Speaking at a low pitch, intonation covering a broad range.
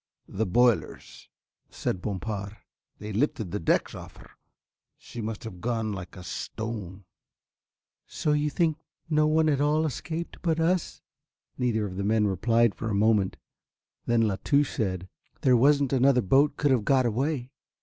Yes: low, 115 Hz; wide, 5.7 semitones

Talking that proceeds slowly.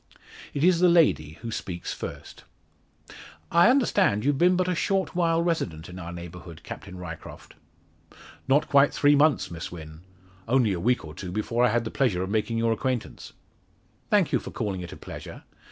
No: average, 185 wpm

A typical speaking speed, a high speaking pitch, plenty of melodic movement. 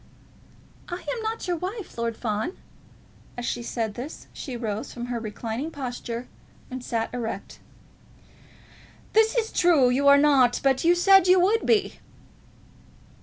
Yes: average, 145 wpm; very high, 265 Hz; wide, 7.1 semitones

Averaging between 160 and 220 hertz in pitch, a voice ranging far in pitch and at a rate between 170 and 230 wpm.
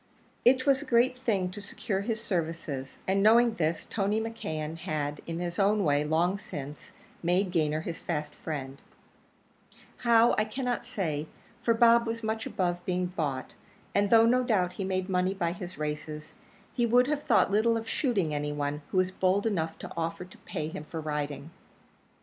Yes: medium, 185 Hz; wide, 6.2 semitones; average, 180 wpm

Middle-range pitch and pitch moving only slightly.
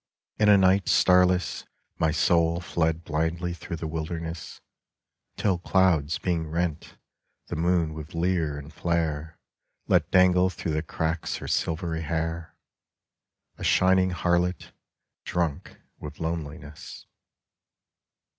No: very low, 85 Hz; narrow, 2.0 semitones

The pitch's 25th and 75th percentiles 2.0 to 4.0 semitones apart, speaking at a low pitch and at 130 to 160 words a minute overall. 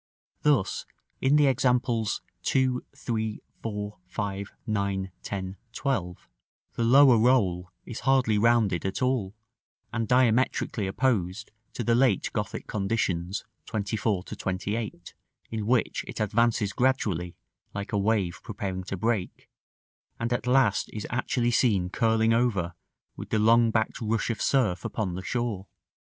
Yes: average, 3.6 semitones; low, 110 Hz; slow, 135 wpm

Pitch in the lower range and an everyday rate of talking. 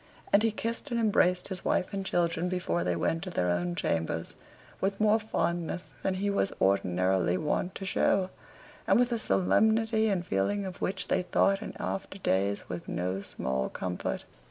No: medium, 180 Hz; average, 180 wpm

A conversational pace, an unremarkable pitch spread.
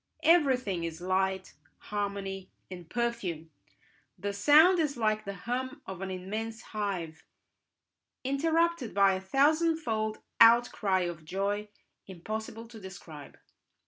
No: slow, 110 wpm; average, 4.5 semitones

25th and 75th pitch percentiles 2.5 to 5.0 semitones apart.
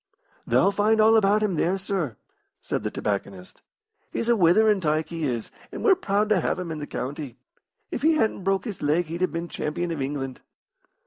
No: wide, 5.6 semitones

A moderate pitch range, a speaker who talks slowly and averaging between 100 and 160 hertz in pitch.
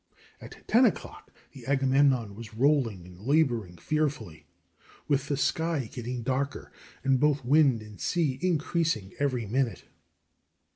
Yes: average, 4.6 semitones; slow, 130 wpm; low, 135 Hz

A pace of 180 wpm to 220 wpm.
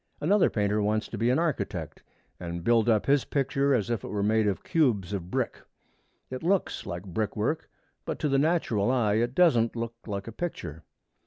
Yes: average, 195 wpm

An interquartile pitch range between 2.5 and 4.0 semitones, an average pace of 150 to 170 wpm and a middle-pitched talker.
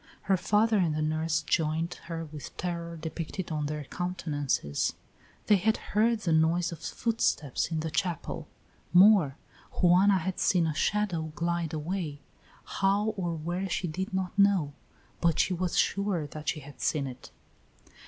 Yes: average, 3.4 semitones; average, 155 wpm; medium, 170 Hz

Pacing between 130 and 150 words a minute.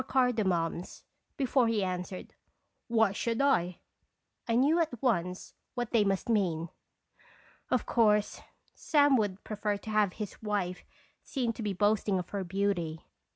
Yes: average, 140 wpm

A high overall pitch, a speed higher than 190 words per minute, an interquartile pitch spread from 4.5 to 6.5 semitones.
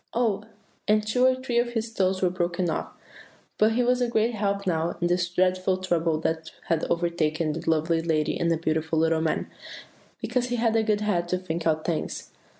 No: medium, 180 Hz; fast, 205 wpm; average, 4.9 semitones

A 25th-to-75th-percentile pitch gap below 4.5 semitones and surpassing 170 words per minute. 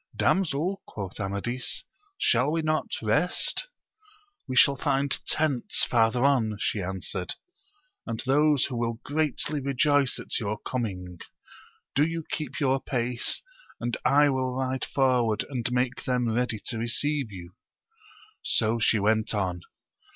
No: average, 4.0 semitones; slow, 135 wpm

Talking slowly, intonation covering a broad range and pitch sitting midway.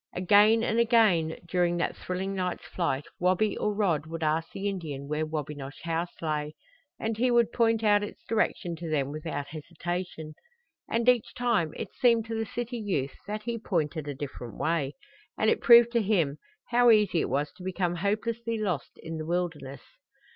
No: average, 180 wpm; wide, 5.9 semitones; medium, 180 Hz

